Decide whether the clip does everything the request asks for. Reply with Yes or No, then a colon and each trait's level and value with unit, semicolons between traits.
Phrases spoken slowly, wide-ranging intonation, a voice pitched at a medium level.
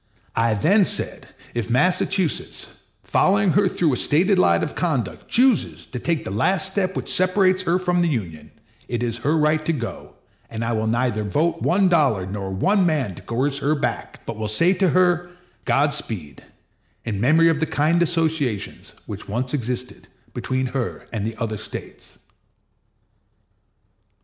No: average, 165 wpm; wide, 7.5 semitones; medium, 145 Hz